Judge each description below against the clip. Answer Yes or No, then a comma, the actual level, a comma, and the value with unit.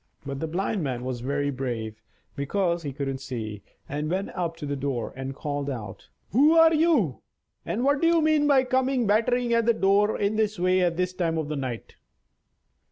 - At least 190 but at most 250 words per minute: Yes, average, 195 wpm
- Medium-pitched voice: Yes, medium, 170 Hz